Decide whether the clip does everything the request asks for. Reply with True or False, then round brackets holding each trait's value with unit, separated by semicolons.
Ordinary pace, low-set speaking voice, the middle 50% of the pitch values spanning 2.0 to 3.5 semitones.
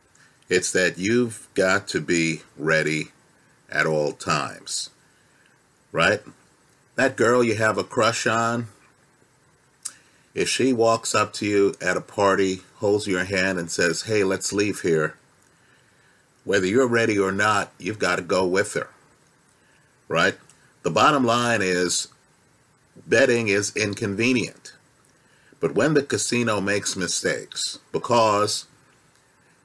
False (125 wpm; 100 Hz; 3.2 semitones)